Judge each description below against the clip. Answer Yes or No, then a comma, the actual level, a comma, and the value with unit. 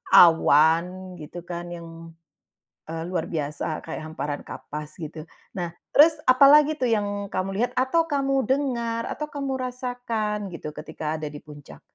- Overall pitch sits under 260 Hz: Yes, medium, 185 Hz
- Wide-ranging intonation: Yes, wide, 7.9 semitones